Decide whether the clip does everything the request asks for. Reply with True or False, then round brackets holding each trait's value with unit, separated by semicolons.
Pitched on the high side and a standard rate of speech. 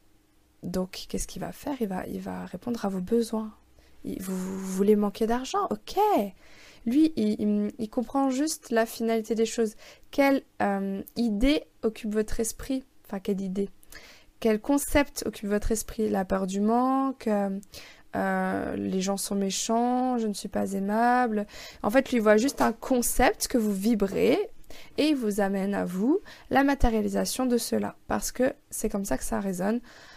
True (220 Hz; 175 wpm)